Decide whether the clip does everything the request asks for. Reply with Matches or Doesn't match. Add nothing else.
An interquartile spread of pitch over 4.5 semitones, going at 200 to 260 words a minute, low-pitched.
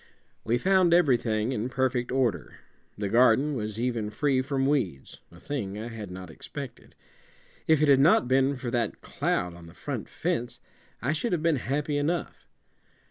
Doesn't match